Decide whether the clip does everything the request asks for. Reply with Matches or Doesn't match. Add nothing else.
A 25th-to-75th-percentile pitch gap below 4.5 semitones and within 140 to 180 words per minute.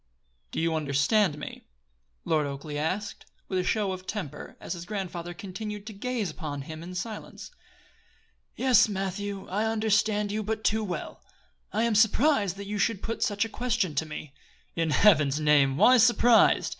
Doesn't match